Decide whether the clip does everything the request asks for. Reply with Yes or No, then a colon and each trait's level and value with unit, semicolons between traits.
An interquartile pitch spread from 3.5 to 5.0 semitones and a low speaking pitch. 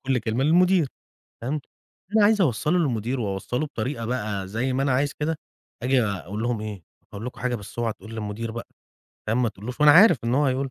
Yes: average, 4.5 semitones; low, 125 Hz